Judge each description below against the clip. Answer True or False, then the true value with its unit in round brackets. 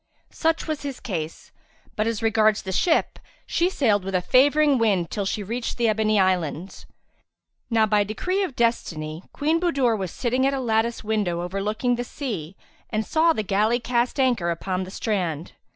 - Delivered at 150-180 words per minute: True (175 wpm)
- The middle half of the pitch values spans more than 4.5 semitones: True (4.9 semitones)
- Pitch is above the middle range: True (220 Hz)